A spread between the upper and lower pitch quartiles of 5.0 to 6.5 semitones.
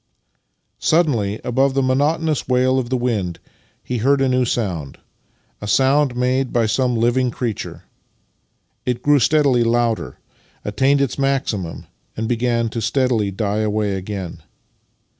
No: average, 3.5 semitones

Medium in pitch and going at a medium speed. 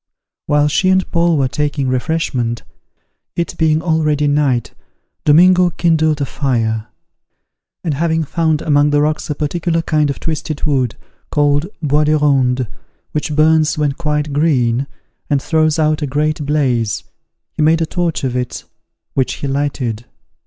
Yes: medium, 150 Hz; average, 150 wpm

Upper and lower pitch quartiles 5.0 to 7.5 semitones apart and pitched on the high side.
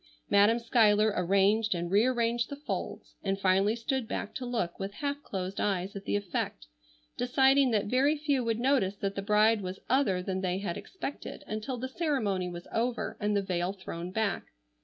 No: average, 4.3 semitones; high, 210 Hz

